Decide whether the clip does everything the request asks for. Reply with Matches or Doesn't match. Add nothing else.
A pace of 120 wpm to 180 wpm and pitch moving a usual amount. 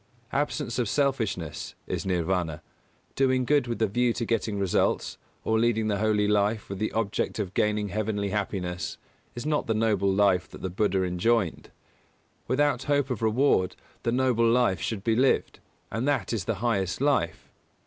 Matches